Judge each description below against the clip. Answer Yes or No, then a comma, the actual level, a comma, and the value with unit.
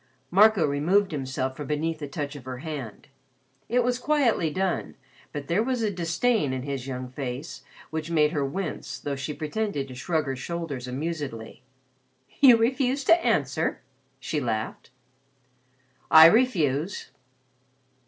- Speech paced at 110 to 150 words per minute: Yes, average, 145 wpm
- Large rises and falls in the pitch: Yes, wide, 6.7 semitones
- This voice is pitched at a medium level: Yes, medium, 155 Hz